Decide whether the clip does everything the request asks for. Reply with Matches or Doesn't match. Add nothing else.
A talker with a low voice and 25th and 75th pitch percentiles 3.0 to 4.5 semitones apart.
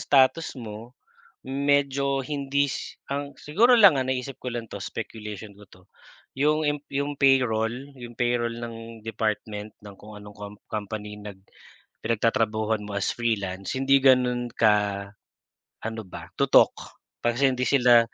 Matches